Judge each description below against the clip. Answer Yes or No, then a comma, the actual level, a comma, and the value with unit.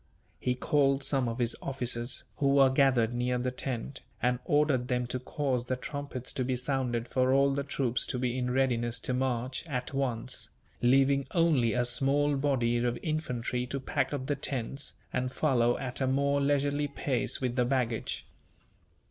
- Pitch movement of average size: No, narrow, 2.1 semitones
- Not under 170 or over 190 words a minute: Yes, average, 175 wpm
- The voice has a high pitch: No, low, 130 Hz